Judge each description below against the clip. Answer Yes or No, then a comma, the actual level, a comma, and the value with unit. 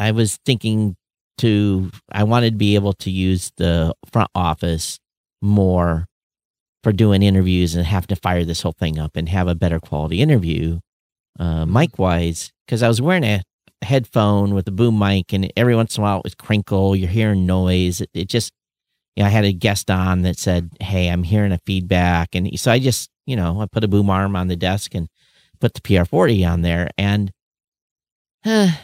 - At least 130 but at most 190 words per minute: No, average, 200 wpm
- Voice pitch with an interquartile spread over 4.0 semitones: No, average, 3.3 semitones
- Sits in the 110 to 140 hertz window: No, very low, 95 Hz